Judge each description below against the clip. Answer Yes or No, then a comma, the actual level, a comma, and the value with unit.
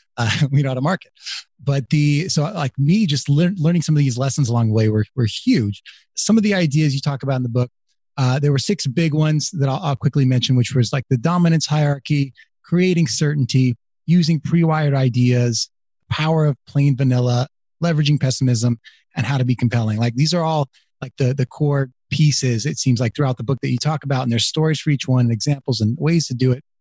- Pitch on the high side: No, medium, 140 Hz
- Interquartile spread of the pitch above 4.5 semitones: No, average, 3.3 semitones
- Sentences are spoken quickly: Yes, fast, 220 wpm